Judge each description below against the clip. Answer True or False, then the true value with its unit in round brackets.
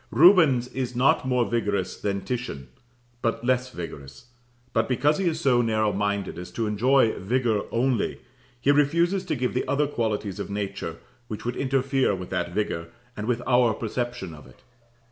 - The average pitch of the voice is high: False (120 Hz)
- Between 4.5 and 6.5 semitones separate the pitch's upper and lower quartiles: False (4.1 semitones)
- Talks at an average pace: True (170 wpm)